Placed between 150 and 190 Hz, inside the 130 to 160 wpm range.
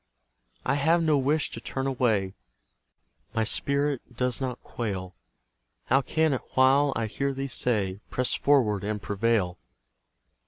No: low, 125 Hz; average, 140 wpm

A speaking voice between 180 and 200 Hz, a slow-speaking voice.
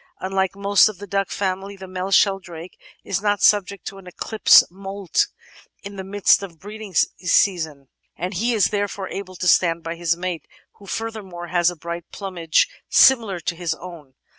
No: high, 190 Hz; average, 180 wpm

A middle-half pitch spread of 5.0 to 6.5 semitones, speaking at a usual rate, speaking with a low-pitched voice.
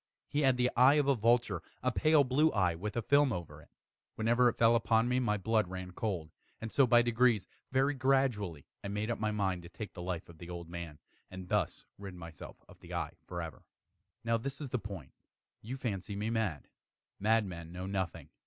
No: wide, 5.4 semitones; fast, 210 wpm; low, 110 Hz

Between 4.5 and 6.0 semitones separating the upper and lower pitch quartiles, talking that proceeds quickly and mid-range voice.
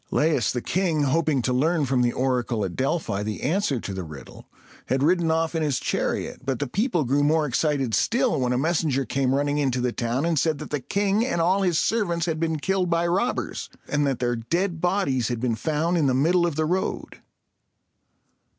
Yes: average, 5.0 semitones; fast, 210 wpm; medium, 150 Hz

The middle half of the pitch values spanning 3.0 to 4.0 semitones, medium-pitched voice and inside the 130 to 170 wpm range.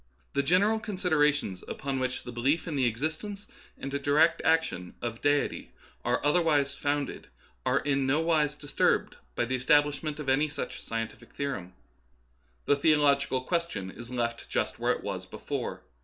Yes: average, 3.4 semitones; medium, 145 Hz; average, 155 wpm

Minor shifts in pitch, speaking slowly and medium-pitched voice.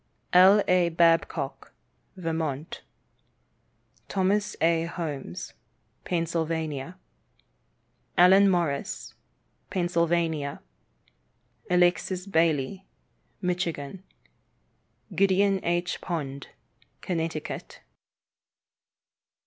Yes: narrow, 2.3 semitones; slow, 55 wpm; medium, 170 Hz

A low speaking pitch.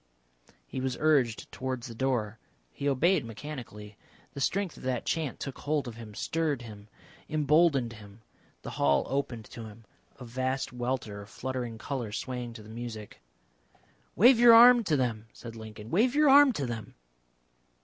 Yes: low, 125 Hz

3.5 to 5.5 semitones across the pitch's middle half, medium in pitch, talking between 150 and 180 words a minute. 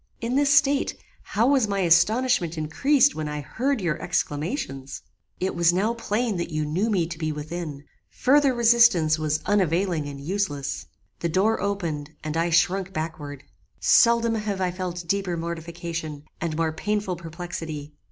Yes: average, 5.2 semitones; medium, 175 Hz; average, 155 wpm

